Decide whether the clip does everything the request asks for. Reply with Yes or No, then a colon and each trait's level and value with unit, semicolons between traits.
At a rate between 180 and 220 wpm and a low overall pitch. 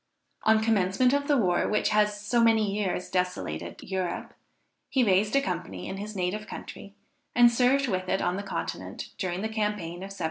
No: average, 185 wpm; high, 205 Hz